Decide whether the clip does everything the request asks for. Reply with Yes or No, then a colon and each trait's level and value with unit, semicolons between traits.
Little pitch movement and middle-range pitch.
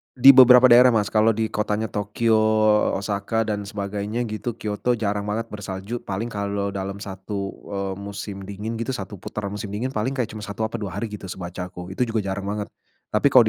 No: narrow, 2.2 semitones; low, 105 Hz